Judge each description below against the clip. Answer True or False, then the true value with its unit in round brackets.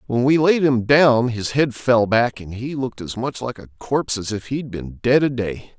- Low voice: True (120 Hz)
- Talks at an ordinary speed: False (260 wpm)